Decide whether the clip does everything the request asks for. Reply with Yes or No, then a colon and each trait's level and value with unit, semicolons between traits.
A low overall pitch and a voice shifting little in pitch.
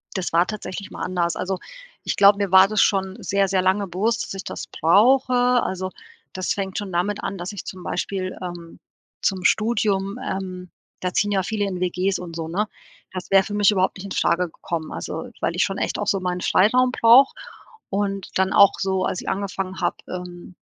No: high, 190 Hz; narrow, 1.8 semitones